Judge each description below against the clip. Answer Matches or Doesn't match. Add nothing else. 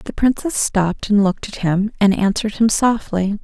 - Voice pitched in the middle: Doesn't match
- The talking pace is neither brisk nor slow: Matches